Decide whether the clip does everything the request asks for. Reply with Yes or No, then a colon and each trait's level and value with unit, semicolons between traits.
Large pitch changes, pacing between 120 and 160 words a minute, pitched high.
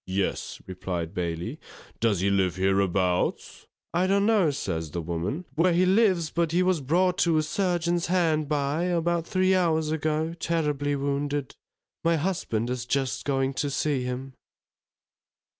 No: wide, 6.9 semitones; average, 150 wpm; medium, 150 Hz